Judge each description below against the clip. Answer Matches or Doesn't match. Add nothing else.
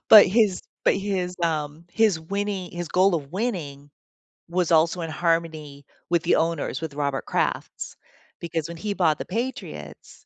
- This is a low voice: Doesn't match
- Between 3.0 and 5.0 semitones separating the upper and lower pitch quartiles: Matches